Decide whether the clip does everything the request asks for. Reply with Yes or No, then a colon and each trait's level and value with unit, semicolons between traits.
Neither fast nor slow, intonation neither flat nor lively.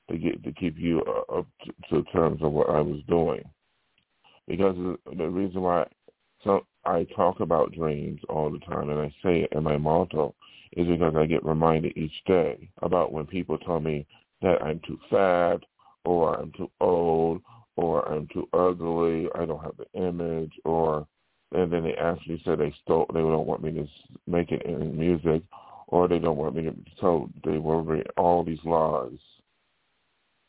No: average, 175 wpm; narrow, 1.8 semitones